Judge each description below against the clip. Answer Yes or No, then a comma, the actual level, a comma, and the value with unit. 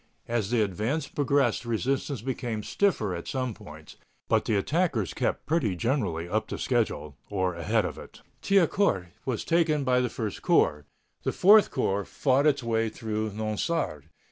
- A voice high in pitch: No, low, 115 Hz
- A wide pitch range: Yes, wide, 5.8 semitones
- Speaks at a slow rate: No, average, 160 wpm